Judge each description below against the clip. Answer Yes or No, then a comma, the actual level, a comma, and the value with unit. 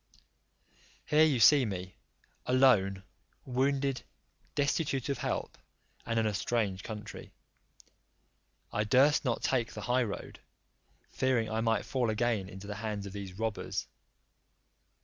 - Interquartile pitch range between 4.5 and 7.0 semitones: No, average, 4.1 semitones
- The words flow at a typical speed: No, slow, 130 wpm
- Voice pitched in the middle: No, low, 115 Hz